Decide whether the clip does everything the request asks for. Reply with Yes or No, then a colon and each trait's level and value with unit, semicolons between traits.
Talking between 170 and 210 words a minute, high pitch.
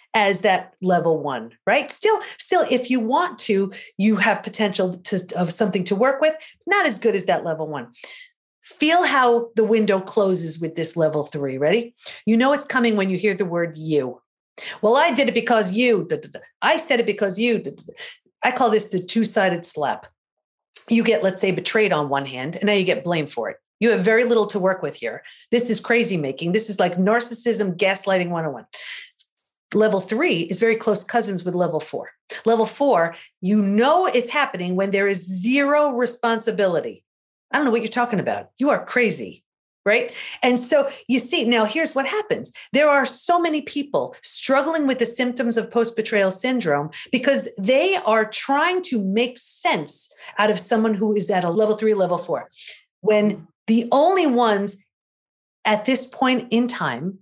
Yes: average, 190 wpm; high, 220 Hz